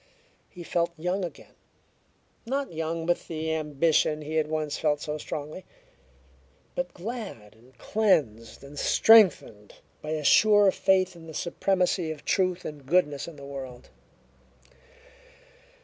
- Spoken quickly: No, slow, 135 wpm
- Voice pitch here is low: No, medium, 160 Hz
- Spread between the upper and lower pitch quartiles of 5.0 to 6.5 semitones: No, average, 3.9 semitones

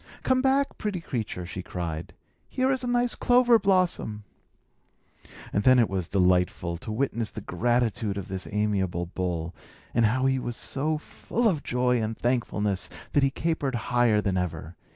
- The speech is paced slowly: No, average, 165 wpm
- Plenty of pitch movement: Yes, wide, 8.1 semitones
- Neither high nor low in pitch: No, low, 115 Hz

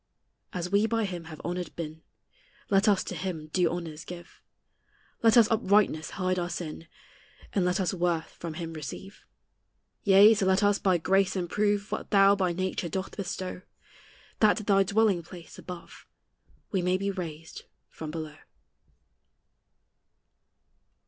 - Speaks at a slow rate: No, average, 150 wpm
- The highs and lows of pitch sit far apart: No, average, 2.8 semitones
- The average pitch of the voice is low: No, medium, 185 Hz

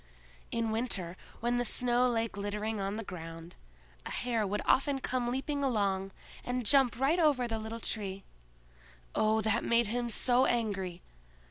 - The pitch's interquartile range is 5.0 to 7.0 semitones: No, average, 3.4 semitones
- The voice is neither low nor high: No, high, 225 Hz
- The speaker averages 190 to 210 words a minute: No, average, 155 wpm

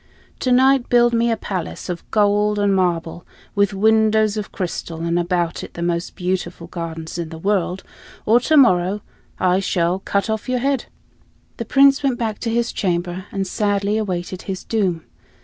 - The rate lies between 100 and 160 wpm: No, average, 170 wpm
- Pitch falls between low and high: No, high, 200 Hz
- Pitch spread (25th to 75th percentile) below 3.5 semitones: No, average, 3.9 semitones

